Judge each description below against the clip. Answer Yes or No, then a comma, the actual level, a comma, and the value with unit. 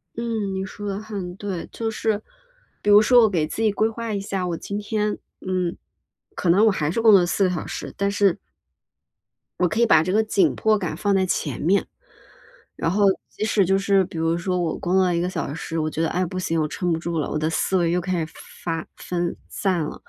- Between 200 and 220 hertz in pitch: No, medium, 185 Hz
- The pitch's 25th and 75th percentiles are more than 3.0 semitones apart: Yes, average, 3.4 semitones